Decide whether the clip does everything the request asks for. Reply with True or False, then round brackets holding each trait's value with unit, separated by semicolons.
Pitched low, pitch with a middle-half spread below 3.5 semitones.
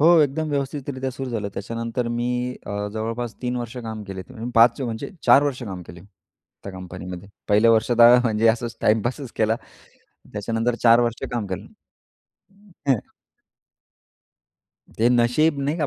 True (115 Hz; 2.5 semitones)